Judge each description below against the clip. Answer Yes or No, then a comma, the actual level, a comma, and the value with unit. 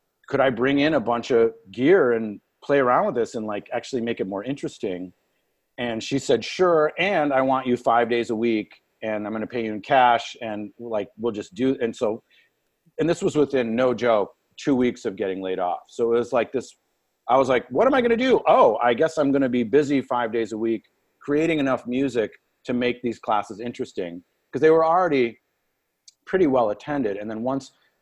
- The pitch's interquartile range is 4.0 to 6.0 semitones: No, average, 3.4 semitones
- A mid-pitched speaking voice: No, low, 120 Hz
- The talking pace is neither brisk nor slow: No, fast, 220 wpm